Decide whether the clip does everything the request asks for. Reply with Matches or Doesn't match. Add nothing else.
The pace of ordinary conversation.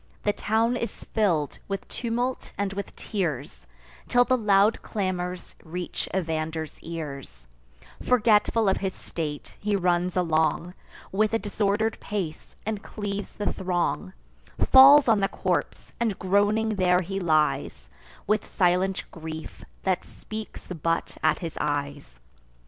Doesn't match